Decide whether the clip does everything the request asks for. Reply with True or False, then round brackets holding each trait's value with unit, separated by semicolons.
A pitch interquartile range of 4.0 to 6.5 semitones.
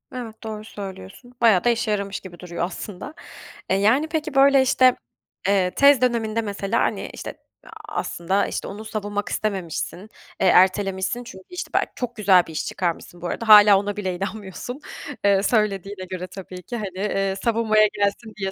False (3.2 semitones)